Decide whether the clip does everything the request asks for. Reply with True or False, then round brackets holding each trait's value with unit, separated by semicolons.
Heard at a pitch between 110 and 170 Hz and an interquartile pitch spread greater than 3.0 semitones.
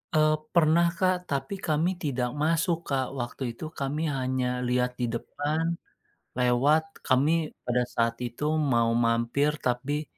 True (135 Hz; 3.9 semitones)